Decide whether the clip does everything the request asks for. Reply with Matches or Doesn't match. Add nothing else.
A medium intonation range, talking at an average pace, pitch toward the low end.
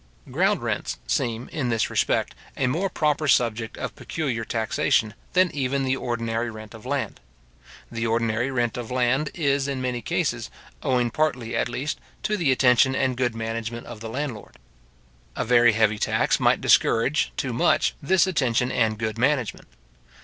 Matches